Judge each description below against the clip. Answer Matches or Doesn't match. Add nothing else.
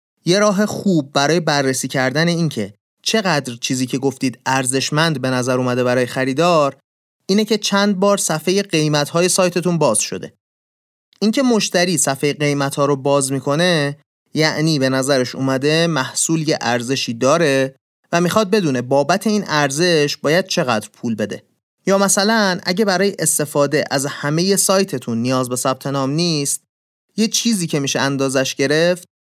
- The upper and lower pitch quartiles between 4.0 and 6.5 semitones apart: Matches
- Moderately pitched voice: Matches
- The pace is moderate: Matches